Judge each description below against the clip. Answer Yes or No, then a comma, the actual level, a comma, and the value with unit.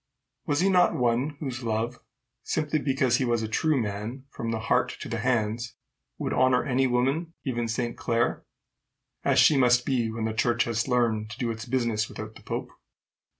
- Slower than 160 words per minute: No, average, 190 wpm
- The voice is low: Yes, low, 120 Hz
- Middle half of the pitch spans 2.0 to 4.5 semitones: Yes, average, 2.7 semitones